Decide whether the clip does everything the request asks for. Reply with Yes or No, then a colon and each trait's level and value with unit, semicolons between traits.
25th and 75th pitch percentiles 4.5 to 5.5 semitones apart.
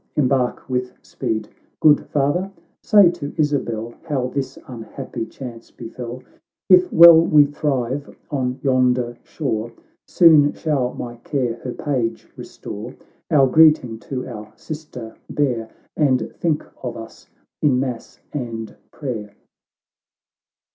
No: average, 3.8 semitones